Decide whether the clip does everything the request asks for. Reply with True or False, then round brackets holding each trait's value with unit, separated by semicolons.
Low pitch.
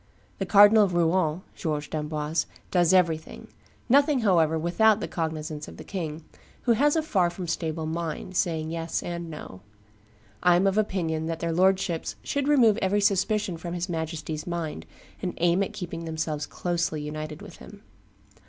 False (170 Hz)